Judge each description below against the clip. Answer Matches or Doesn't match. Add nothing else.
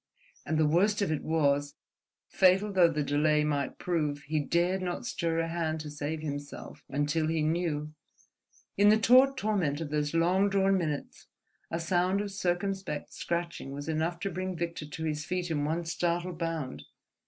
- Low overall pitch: Doesn't match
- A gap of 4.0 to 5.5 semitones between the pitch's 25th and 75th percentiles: Doesn't match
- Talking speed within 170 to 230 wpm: Matches